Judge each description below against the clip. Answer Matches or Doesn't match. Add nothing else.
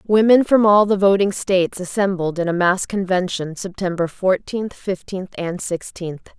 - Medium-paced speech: Matches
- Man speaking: Doesn't match